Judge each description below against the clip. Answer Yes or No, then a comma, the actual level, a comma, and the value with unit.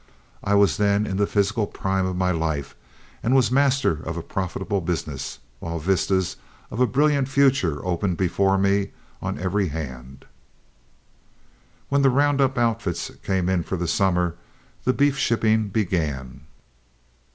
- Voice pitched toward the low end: Yes, very low, 95 Hz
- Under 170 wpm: Yes, average, 150 wpm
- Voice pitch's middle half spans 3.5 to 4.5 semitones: No, average, 5.3 semitones